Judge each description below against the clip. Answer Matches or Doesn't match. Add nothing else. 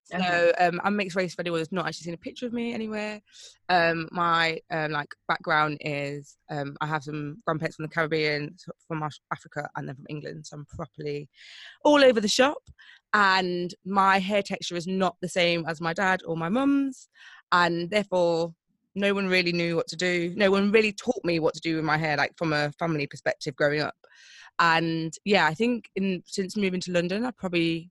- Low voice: Doesn't match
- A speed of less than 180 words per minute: Doesn't match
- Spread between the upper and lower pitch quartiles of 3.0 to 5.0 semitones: Matches